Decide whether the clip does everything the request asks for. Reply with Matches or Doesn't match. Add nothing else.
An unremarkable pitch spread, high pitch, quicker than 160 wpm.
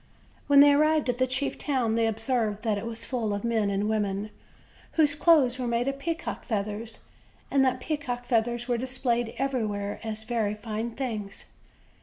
Matches